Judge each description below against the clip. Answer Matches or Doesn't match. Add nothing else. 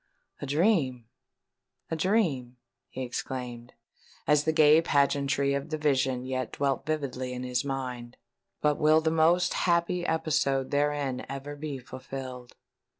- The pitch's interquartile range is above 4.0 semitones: Doesn't match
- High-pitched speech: Doesn't match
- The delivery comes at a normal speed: Doesn't match